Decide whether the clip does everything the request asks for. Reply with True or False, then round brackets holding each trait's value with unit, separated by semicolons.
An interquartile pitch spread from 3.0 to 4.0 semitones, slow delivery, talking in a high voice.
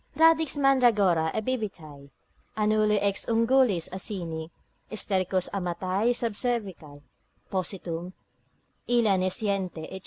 False (4.4 semitones; 90 wpm; 200 Hz)